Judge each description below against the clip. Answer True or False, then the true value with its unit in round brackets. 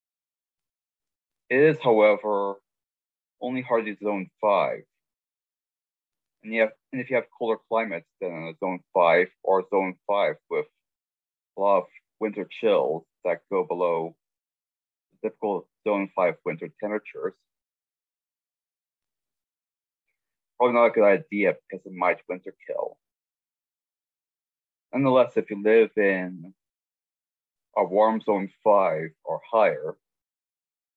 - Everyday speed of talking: False (110 wpm)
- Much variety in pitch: True (5.8 semitones)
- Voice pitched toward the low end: True (105 Hz)